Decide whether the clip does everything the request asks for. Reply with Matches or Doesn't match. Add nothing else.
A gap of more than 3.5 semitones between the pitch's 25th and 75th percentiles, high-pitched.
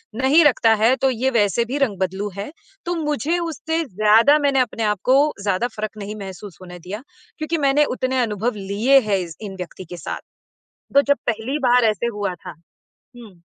Matches